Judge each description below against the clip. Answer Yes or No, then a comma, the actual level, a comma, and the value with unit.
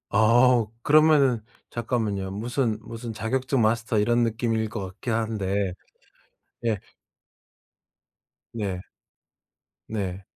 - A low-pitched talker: Yes, low, 115 Hz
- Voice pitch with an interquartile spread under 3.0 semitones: Yes, narrow, 2.6 semitones